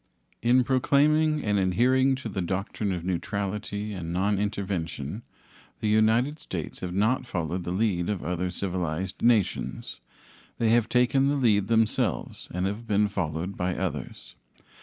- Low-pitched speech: Yes, low, 100 Hz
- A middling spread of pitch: Yes, average, 4.3 semitones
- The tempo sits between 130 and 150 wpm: Yes, average, 140 wpm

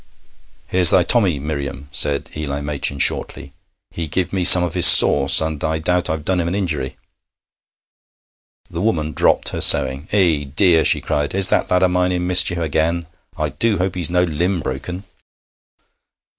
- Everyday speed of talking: Yes, average, 170 wpm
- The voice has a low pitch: Yes, very low, 85 Hz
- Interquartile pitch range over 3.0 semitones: Yes, average, 3.5 semitones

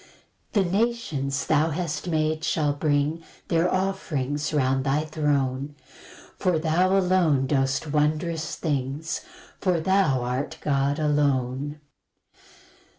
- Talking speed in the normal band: No, slow, 110 wpm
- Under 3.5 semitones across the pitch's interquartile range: Yes, average, 3.1 semitones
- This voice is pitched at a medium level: Yes, medium, 150 Hz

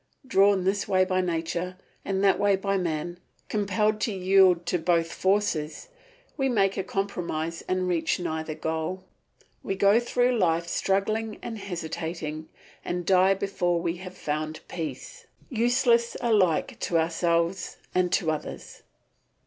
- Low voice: No, medium, 185 Hz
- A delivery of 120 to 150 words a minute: Yes, average, 140 wpm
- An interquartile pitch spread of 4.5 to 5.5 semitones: No, average, 3.1 semitones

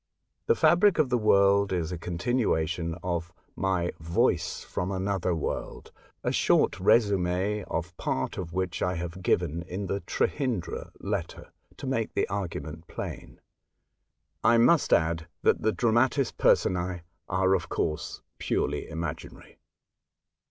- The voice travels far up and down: No, average, 3.7 semitones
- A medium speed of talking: No, slow, 130 wpm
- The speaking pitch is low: Yes, very low, 95 Hz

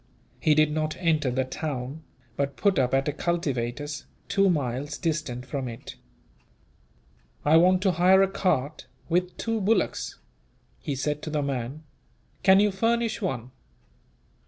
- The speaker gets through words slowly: No, average, 145 wpm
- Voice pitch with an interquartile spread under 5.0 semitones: No, average, 5.3 semitones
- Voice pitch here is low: No, medium, 155 Hz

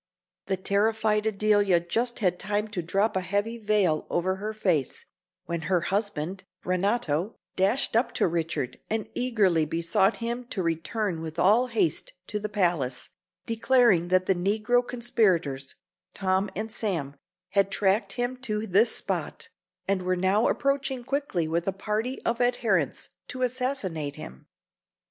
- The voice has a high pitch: Yes, high, 200 Hz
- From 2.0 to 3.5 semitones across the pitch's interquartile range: No, average, 4.4 semitones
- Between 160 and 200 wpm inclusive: No, average, 145 wpm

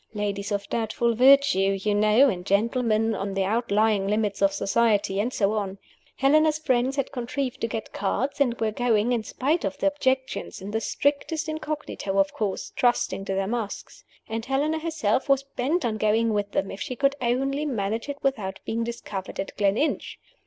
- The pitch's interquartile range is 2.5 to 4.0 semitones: No, average, 5.1 semitones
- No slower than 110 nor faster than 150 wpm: No, average, 180 wpm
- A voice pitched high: Yes, high, 230 Hz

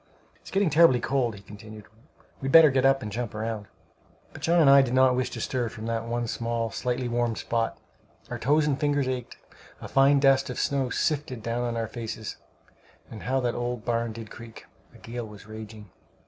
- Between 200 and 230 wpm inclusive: Yes, fast, 205 wpm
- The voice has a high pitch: No, low, 120 Hz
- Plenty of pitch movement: No, average, 3.0 semitones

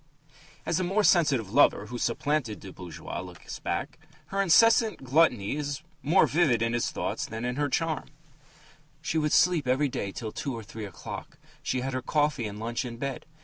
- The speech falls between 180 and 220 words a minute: Yes, average, 185 wpm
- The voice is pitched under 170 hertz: Yes, low, 135 Hz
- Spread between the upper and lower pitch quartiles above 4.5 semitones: Yes, average, 5.1 semitones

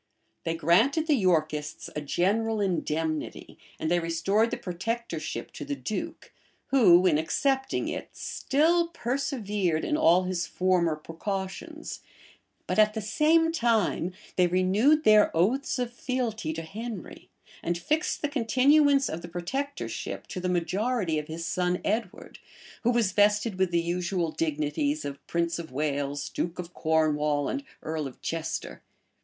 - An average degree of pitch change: No, wide, 6.4 semitones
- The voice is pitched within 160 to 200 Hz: Yes, medium, 185 Hz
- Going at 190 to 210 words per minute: No, average, 145 wpm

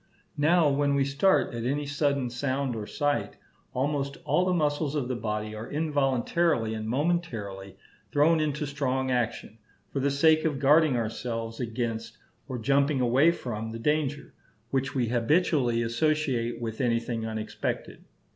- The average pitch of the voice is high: No, low, 135 Hz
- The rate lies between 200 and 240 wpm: No, average, 145 wpm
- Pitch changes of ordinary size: Yes, average, 4.0 semitones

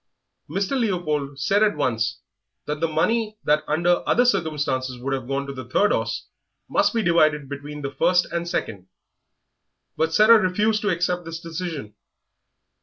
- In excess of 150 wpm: Yes, average, 160 wpm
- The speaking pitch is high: No, medium, 160 Hz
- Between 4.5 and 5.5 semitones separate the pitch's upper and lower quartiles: Yes, average, 5.0 semitones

